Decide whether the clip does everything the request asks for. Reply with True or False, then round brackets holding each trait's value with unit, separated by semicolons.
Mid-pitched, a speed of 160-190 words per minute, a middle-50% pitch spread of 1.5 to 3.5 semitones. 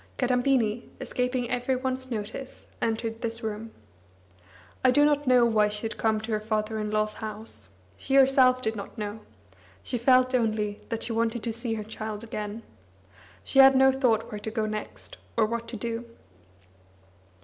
False (230 Hz; 170 wpm; 2.8 semitones)